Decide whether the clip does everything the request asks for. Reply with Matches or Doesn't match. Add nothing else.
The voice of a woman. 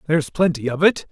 Doesn't match